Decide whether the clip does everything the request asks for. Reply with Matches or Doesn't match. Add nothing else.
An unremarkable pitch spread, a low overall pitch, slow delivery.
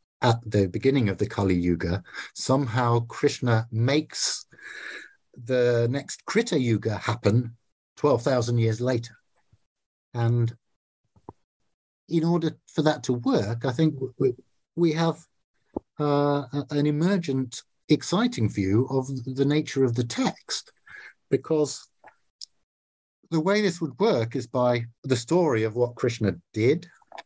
Matches